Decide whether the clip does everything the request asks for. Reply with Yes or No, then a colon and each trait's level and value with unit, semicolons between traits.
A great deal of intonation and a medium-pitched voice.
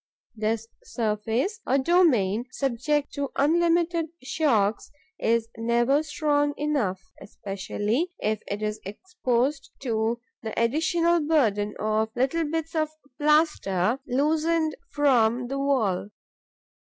No: wide, 5.9 semitones; very high, 265 Hz